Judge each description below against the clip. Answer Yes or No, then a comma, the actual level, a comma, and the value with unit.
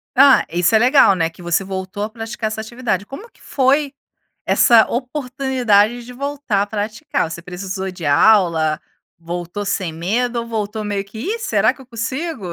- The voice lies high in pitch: Yes, high, 220 Hz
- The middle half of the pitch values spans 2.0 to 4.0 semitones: No, average, 5.0 semitones